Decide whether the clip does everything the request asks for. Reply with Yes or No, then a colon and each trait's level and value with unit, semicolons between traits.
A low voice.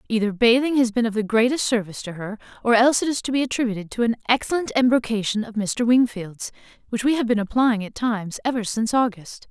No: high, 230 Hz